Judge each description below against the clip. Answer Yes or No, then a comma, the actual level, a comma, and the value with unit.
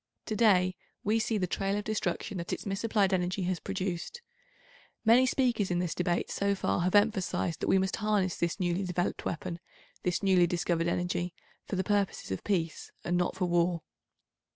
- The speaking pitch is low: No, medium, 185 Hz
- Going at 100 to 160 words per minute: No, average, 180 wpm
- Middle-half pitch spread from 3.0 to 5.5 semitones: No, narrow, 2.6 semitones